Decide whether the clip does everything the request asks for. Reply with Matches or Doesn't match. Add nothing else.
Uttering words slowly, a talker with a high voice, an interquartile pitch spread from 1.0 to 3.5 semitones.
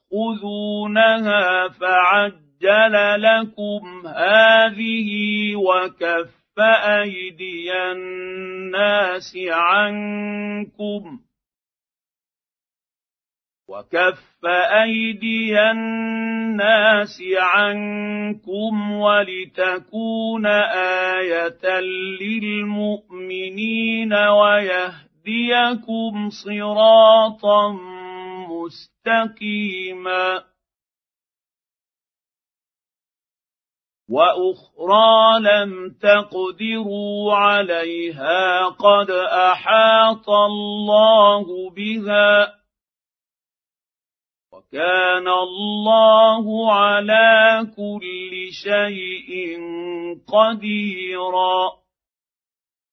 Matches